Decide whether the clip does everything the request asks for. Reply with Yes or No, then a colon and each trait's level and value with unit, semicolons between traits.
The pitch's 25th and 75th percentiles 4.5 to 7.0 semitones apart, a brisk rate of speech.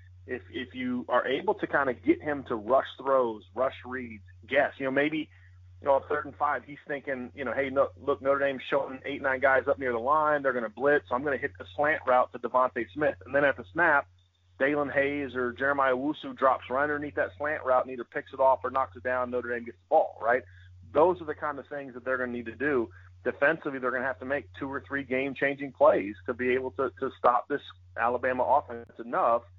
No: average, 3.0 semitones; fast, 250 wpm